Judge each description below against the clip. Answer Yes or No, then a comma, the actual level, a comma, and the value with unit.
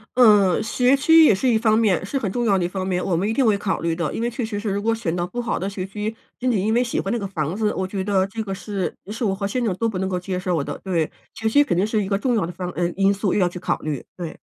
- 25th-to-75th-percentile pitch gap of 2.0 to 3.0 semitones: No, average, 3.5 semitones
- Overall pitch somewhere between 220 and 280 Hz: No, high, 200 Hz